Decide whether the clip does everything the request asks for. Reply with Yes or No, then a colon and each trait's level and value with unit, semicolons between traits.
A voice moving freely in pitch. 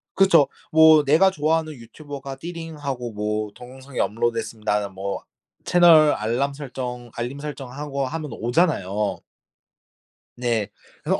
No: average, 4.7 semitones